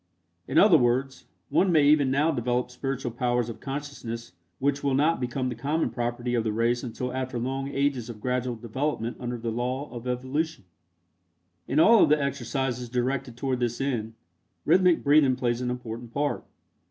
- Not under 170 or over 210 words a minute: Yes, average, 175 wpm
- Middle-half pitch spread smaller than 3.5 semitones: Yes, narrow, 2.5 semitones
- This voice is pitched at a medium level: No, low, 125 Hz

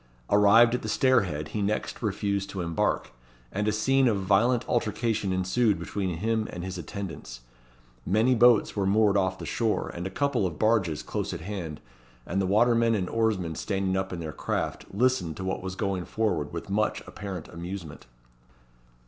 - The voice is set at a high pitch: No, low, 100 Hz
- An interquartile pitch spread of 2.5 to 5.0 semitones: Yes, average, 3.3 semitones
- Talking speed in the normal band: Yes, average, 175 wpm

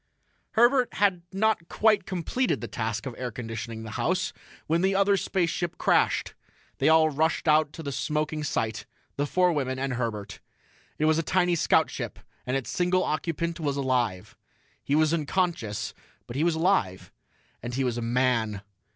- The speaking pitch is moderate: Yes, medium, 155 Hz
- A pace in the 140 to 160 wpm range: No, average, 170 wpm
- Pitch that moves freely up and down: Yes, wide, 6.2 semitones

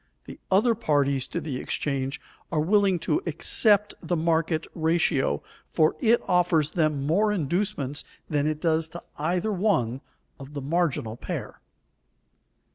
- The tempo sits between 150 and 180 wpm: No, slow, 135 wpm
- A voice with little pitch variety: No, average, 4.1 semitones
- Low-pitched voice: No, medium, 160 Hz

